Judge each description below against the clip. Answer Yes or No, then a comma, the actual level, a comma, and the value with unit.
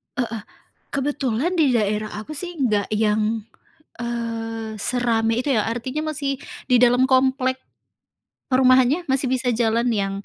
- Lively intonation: No, average, 2.8 semitones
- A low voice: No, high, 245 Hz